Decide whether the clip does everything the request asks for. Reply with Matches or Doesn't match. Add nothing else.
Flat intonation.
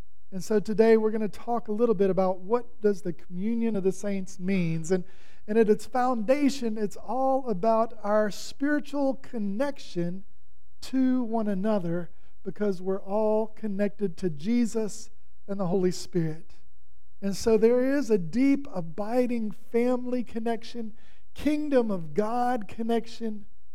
Doesn't match